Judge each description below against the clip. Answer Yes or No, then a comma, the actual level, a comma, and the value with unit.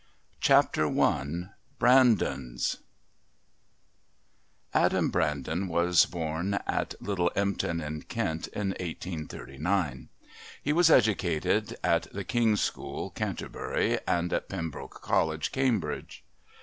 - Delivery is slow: Yes, slow, 95 wpm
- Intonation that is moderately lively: Yes, average, 4.3 semitones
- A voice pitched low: Yes, very low, 85 Hz